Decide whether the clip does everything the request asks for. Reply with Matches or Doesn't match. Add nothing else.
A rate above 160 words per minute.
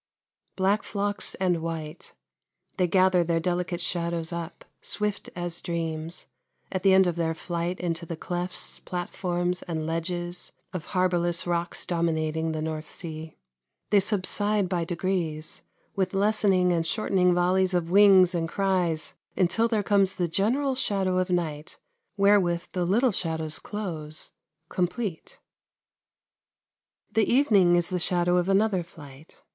Doesn't match